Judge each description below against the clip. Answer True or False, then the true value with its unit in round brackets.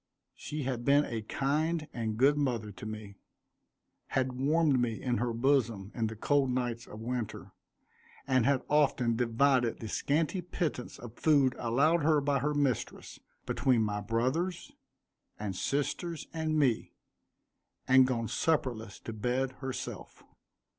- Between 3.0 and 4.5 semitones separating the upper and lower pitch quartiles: True (3.9 semitones)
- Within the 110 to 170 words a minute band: True (140 wpm)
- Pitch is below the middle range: True (130 Hz)